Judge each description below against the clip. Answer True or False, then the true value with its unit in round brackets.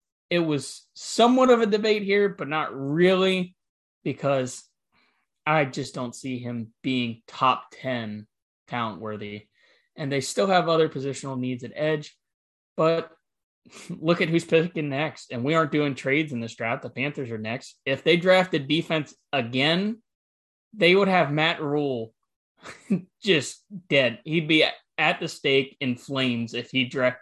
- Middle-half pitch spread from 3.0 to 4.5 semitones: False (4.9 semitones)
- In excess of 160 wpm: False (155 wpm)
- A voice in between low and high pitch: True (145 Hz)